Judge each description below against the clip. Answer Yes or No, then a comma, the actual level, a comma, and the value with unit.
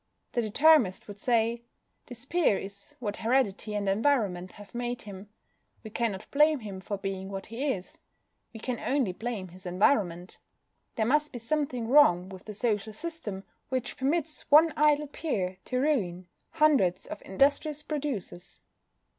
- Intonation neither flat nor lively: No, wide, 6.5 semitones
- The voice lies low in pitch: No, high, 225 Hz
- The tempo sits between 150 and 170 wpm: Yes, average, 155 wpm